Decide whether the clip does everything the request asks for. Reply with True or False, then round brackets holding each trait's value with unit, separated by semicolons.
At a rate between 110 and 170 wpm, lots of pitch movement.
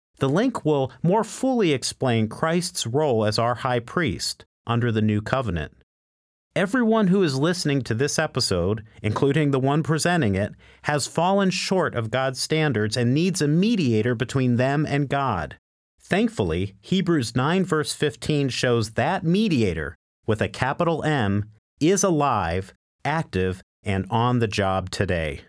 True (145 wpm; 6.9 semitones)